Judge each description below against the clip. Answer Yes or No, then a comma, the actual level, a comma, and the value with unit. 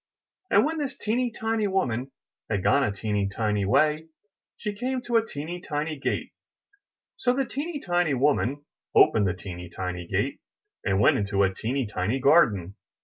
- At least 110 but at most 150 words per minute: No, average, 165 wpm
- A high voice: No, medium, 140 Hz